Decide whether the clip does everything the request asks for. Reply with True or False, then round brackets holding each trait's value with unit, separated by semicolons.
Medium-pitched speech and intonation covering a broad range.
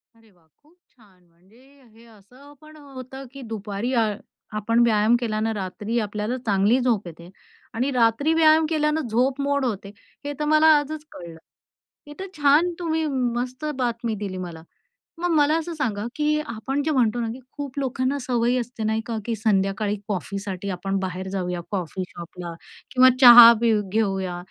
False (230 Hz; 5.8 semitones)